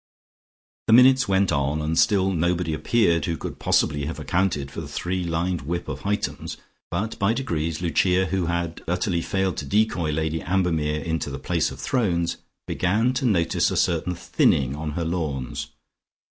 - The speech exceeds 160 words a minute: Yes, average, 170 wpm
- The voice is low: Yes, very low, 85 Hz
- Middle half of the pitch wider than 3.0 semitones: Yes, average, 3.4 semitones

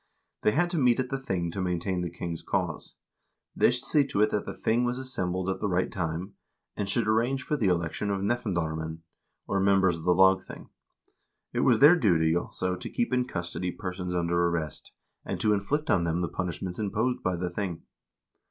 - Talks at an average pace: No, fast, 210 wpm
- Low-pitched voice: Yes, very low, 95 Hz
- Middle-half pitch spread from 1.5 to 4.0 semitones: No, average, 5.1 semitones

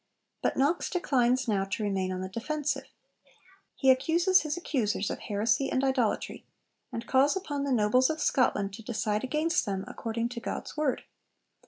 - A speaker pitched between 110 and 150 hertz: No, very high, 255 Hz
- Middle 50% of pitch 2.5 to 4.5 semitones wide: No, wide, 5.6 semitones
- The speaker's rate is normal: Yes, average, 165 wpm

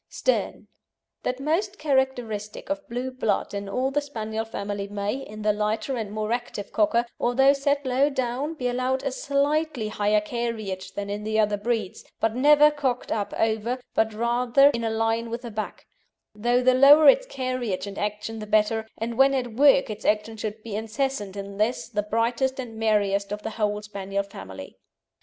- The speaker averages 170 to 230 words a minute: Yes, average, 185 wpm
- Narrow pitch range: No, average, 3.8 semitones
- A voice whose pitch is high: Yes, high, 225 Hz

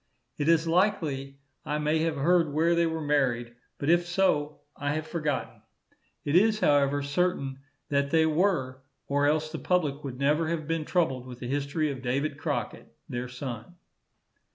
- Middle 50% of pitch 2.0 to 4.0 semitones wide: Yes, average, 3.0 semitones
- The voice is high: No, medium, 150 Hz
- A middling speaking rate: Yes, average, 170 wpm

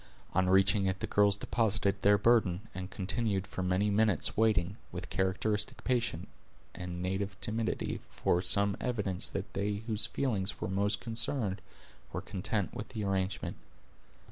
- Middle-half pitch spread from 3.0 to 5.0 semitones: No, narrow, 2.5 semitones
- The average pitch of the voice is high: No, low, 100 Hz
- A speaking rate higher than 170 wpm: No, average, 145 wpm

